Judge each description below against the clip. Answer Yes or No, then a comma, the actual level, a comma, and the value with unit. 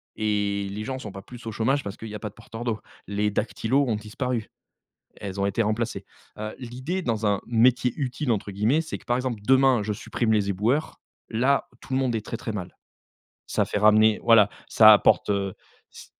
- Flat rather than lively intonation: No, average, 3.1 semitones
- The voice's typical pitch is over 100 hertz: Yes, low, 110 Hz